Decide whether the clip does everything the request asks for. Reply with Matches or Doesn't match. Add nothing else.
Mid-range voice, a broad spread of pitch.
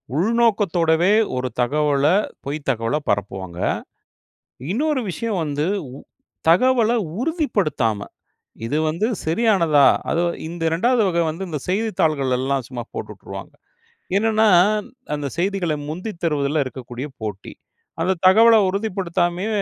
Matches